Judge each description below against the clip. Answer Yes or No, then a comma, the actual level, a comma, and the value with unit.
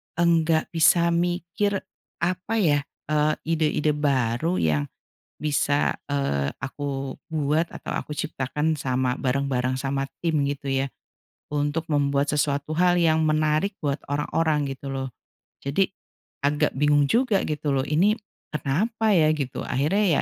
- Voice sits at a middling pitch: Yes, medium, 150 Hz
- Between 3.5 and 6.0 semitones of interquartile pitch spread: No, average, 3.0 semitones